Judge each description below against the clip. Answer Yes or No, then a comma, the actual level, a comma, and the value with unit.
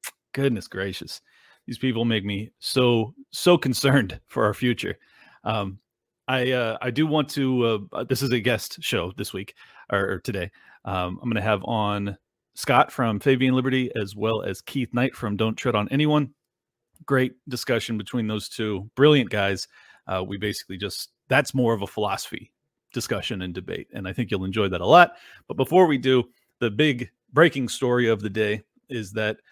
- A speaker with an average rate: Yes, average, 185 wpm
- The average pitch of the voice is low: Yes, low, 115 Hz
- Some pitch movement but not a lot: Yes, average, 3.8 semitones